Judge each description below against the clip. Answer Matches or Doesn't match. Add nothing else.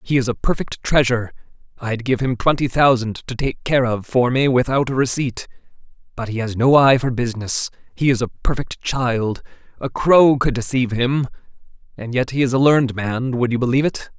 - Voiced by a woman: Doesn't match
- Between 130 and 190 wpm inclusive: Doesn't match